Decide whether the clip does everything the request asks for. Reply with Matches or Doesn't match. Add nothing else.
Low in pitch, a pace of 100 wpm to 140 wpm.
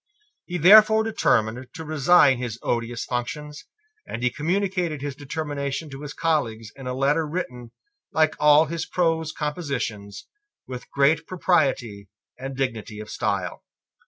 Doesn't match